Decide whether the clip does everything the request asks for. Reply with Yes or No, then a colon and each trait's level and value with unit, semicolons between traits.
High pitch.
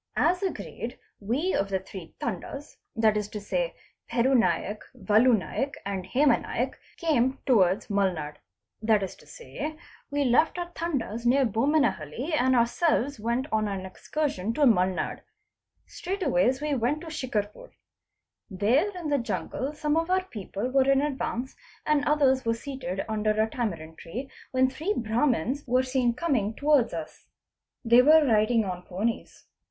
Yes: high, 245 Hz